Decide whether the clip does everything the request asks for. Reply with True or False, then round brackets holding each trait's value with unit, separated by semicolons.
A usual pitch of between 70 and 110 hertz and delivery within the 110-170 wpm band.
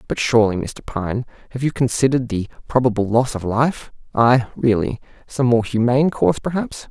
False (120 Hz; 150 wpm)